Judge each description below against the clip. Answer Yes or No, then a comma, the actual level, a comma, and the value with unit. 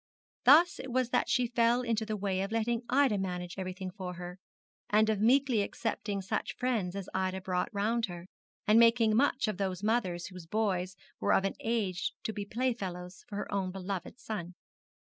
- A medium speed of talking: Yes, average, 190 wpm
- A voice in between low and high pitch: No, high, 205 Hz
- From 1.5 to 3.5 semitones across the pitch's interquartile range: No, average, 3.9 semitones